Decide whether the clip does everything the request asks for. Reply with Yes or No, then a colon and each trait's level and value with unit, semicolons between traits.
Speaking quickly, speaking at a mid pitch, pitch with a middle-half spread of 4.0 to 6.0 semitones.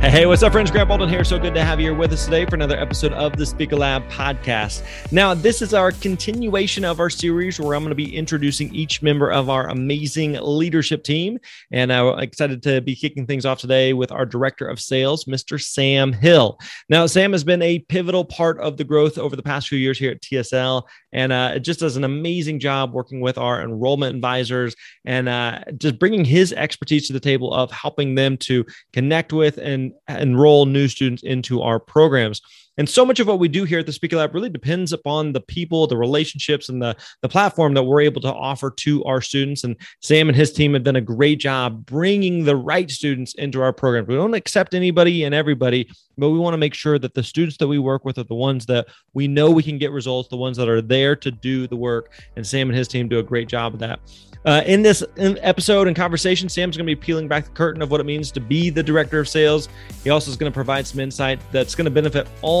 No: fast, 240 wpm; medium, 145 Hz; average, 3.4 semitones